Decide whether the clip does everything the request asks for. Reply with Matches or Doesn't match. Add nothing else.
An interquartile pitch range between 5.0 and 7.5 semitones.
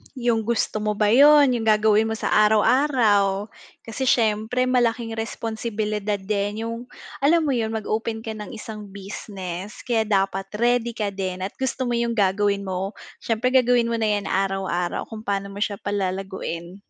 Doesn't match